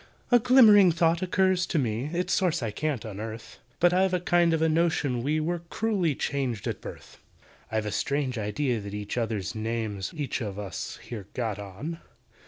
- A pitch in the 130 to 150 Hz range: Yes, medium, 140 Hz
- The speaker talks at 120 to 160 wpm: No, average, 190 wpm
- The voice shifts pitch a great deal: Yes, wide, 7.9 semitones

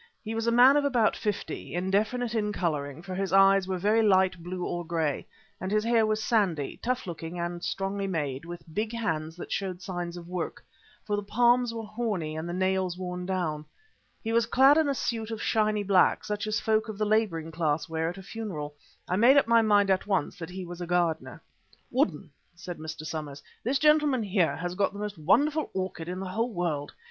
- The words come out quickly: Yes, fast, 215 wpm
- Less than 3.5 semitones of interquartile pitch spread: No, average, 4.2 semitones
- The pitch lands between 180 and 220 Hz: Yes, high, 190 Hz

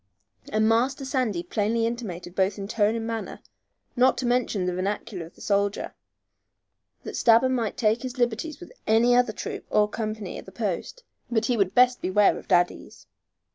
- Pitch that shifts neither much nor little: Yes, average, 3.3 semitones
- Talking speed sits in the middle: Yes, average, 170 wpm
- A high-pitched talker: Yes, high, 220 Hz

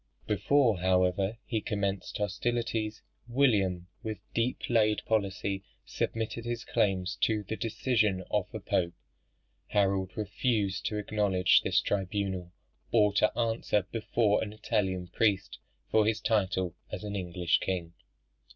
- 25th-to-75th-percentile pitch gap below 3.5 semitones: Yes, average, 2.9 semitones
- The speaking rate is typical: No, slow, 125 wpm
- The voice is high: No, low, 105 Hz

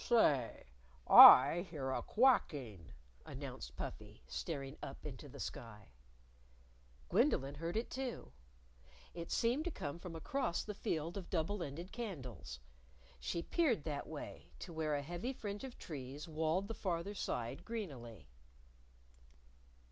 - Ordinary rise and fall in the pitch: No, wide, 7.0 semitones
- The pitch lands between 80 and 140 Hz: No, medium, 165 Hz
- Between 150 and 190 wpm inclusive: No, slow, 135 wpm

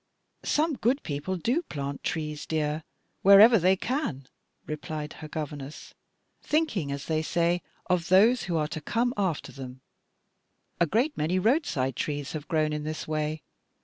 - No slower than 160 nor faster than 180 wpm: No, average, 150 wpm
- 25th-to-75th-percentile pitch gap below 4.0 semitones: No, average, 5.2 semitones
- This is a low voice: No, medium, 160 Hz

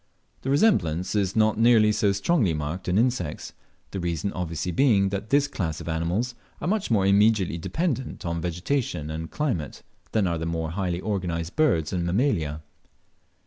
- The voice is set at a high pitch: No, very low, 95 Hz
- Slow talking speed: No, average, 165 wpm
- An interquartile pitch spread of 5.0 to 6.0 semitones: Yes, average, 5.3 semitones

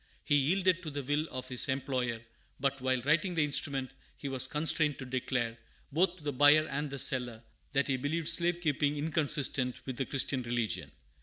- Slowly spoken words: No, average, 185 wpm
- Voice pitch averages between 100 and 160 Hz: Yes, medium, 140 Hz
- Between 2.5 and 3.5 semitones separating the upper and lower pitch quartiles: Yes, average, 3.0 semitones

